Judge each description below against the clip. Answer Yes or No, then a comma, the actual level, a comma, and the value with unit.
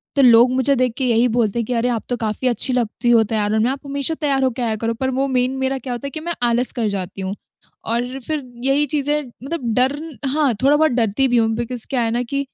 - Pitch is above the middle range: Yes, very high, 250 Hz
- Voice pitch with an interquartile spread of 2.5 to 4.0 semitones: Yes, average, 2.8 semitones